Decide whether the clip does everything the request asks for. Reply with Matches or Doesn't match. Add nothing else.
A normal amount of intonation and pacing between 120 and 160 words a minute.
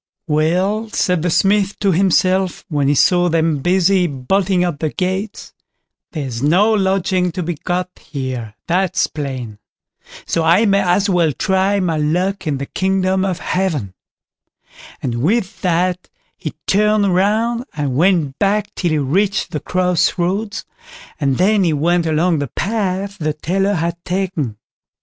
Matches